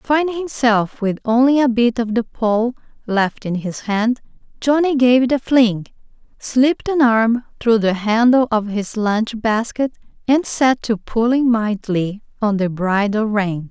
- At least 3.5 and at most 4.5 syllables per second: Yes, 4.1 syllables/s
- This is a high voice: Yes, high, 230 Hz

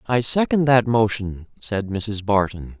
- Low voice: Yes, low, 110 Hz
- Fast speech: No, average, 150 wpm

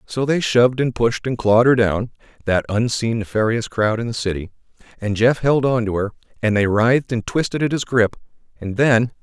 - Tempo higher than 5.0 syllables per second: Yes, 5.4 syllables/s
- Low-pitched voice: Yes, low, 115 Hz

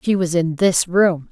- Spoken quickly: Yes, fast, 230 wpm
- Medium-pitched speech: Yes, medium, 175 Hz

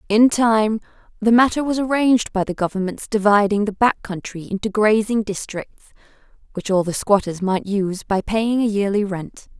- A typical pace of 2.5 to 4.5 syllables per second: No, 5.0 syllables/s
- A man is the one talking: No, female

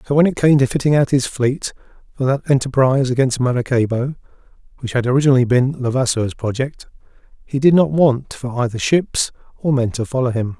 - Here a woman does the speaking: No, male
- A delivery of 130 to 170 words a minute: No, average, 180 wpm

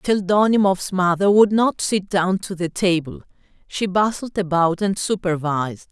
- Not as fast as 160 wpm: Yes, average, 140 wpm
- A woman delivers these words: Yes, female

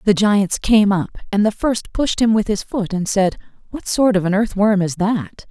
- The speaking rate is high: Yes, fast, 230 wpm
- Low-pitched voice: No, high, 205 Hz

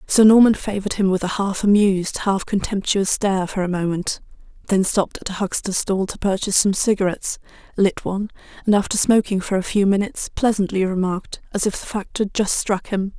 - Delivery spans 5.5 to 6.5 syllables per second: Yes, 5.8 syllables/s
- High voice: Yes, high, 195 Hz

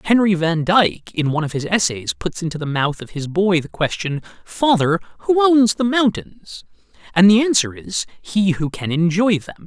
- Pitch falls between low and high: Yes, medium, 180 Hz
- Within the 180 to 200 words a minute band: Yes, average, 195 wpm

